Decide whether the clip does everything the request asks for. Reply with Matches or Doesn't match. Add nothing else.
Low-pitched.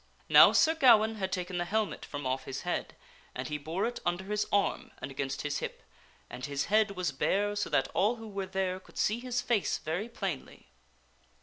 Doesn't match